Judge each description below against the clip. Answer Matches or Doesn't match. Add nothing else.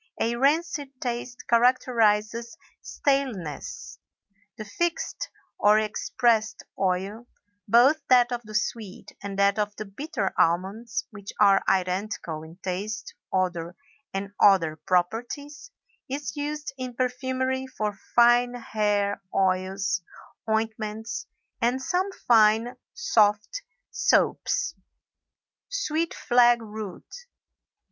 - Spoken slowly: Matches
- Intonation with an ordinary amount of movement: Matches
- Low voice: Doesn't match